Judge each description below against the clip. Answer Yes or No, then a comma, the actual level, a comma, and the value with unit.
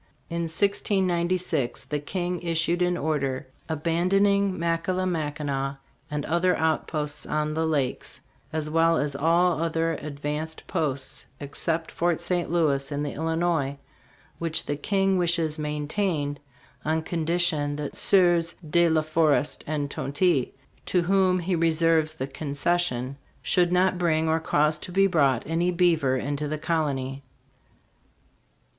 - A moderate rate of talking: No, slow, 130 wpm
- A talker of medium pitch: Yes, medium, 160 Hz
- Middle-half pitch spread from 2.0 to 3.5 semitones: Yes, average, 2.9 semitones